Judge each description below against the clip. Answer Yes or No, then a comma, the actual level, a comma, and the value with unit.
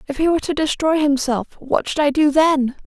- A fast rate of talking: Yes, fast, 230 wpm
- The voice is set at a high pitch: Yes, very high, 290 Hz